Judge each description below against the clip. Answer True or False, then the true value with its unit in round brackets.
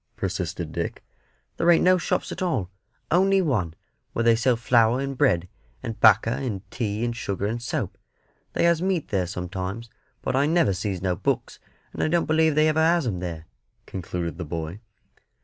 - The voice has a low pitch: True (115 Hz)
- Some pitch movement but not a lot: False (8.8 semitones)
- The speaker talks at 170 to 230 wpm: True (185 wpm)